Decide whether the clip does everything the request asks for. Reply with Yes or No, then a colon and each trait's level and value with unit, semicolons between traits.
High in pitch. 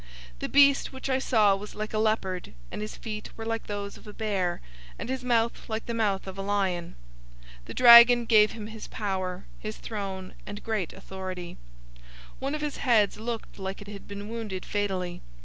Yes: high, 210 Hz